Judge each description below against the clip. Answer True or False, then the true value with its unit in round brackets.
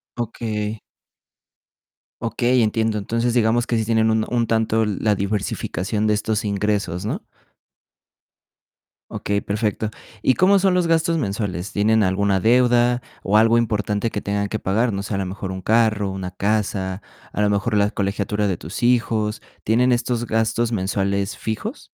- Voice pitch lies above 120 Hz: False (110 Hz)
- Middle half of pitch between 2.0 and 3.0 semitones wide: True (2.5 semitones)